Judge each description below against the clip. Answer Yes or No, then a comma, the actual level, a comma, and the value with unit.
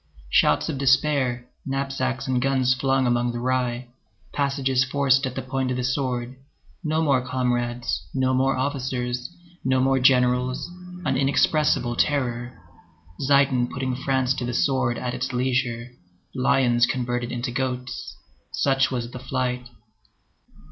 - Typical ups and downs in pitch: No, narrow, 1.4 semitones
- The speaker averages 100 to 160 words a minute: Yes, slow, 135 wpm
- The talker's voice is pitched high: No, low, 130 Hz